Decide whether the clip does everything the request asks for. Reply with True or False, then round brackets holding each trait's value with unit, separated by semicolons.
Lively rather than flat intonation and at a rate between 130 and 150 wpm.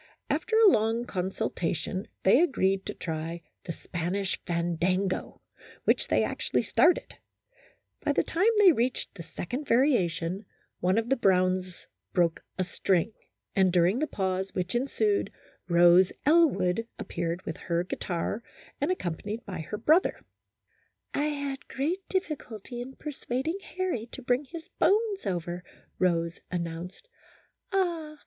True (8.3 semitones; 140 wpm)